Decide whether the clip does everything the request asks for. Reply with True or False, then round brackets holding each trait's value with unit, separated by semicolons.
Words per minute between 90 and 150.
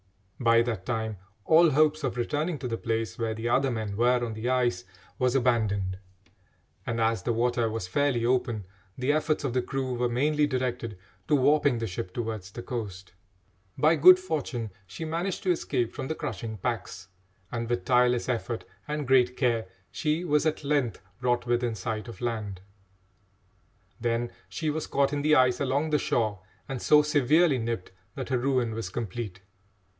False (175 wpm)